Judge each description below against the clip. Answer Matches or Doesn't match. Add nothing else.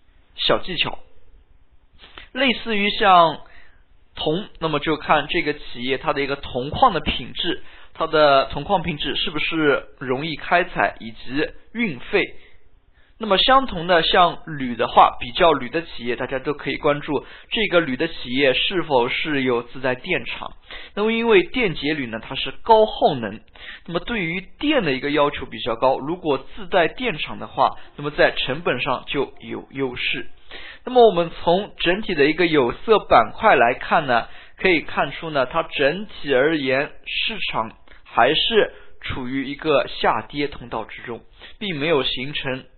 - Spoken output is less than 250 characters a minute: Matches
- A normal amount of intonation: Doesn't match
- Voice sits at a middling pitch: Matches